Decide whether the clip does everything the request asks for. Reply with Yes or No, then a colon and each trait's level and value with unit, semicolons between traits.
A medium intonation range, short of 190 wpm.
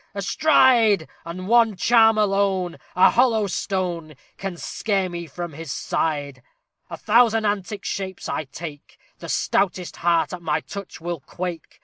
Yes: average, 3.8 semitones; average, 140 wpm